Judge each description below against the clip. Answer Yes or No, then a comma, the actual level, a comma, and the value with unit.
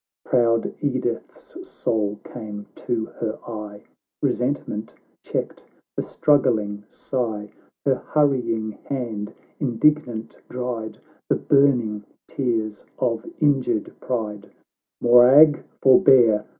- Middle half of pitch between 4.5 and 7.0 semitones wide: No, average, 3.4 semitones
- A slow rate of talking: Yes, slow, 105 wpm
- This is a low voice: Yes, low, 120 Hz